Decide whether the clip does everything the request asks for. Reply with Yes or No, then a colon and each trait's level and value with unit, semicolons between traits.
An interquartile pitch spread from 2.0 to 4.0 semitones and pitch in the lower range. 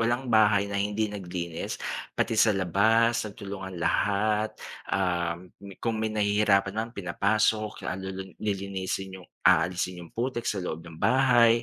Yes: average, 2.9 semitones; low, 100 Hz